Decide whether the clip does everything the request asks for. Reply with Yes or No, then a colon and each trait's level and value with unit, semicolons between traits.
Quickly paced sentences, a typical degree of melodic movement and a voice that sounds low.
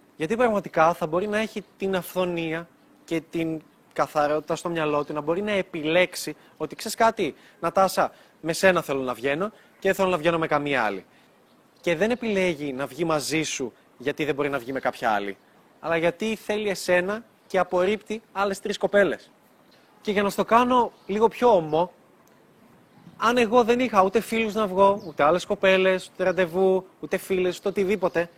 No: fast, 175 wpm; average, 4.2 semitones; medium, 185 Hz